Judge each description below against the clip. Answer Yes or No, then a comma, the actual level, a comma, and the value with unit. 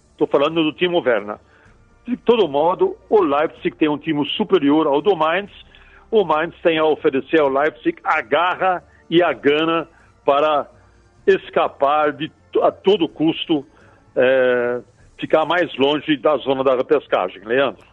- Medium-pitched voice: Yes, medium, 165 Hz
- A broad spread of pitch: Yes, wide, 8.7 semitones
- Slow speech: No, average, 145 wpm